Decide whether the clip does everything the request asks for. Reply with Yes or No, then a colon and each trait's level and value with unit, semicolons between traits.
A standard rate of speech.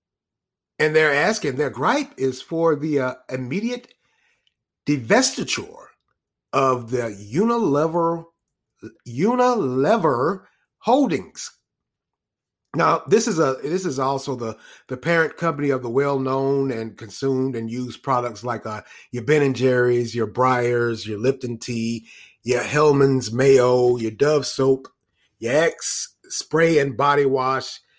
No: slow, 125 wpm